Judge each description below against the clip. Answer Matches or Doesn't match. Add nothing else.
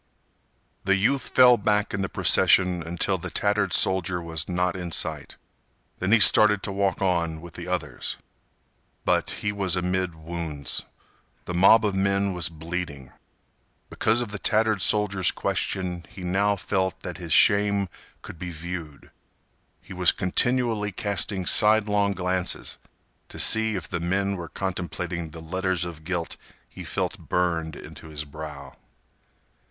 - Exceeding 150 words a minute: Doesn't match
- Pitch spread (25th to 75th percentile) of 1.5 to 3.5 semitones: Matches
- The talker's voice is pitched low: Matches